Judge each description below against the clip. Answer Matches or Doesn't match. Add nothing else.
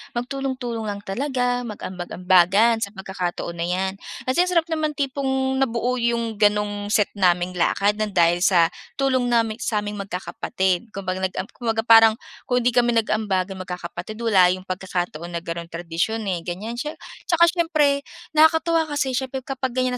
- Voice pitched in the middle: Doesn't match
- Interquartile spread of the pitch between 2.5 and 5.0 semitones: Doesn't match